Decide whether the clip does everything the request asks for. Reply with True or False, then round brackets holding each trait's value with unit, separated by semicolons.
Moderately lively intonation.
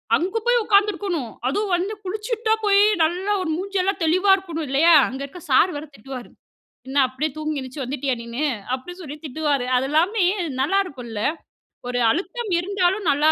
False (6.2 semitones)